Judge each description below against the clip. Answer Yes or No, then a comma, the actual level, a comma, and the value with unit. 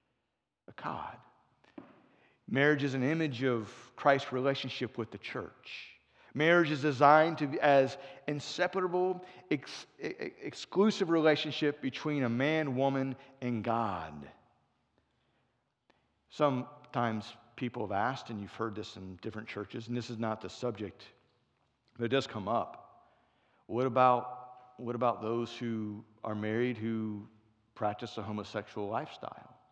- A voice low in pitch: Yes, low, 125 Hz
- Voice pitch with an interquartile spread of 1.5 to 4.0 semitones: No, average, 4.8 semitones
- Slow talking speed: Yes, slow, 125 wpm